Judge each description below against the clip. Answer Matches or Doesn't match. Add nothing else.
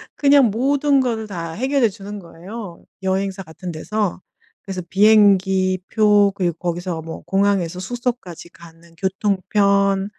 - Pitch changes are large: Doesn't match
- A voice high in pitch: Matches